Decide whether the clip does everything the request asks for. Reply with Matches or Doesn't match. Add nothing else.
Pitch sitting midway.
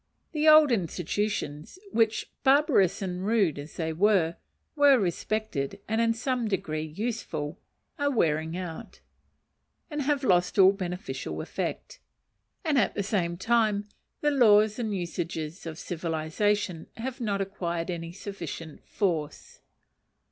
Doesn't match